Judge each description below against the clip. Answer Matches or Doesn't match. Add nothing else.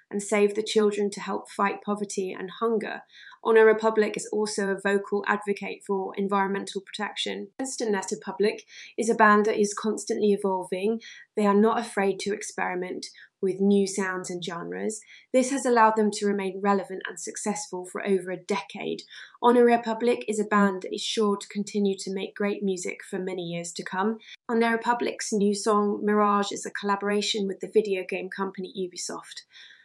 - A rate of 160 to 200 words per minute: Matches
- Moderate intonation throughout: Doesn't match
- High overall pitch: Matches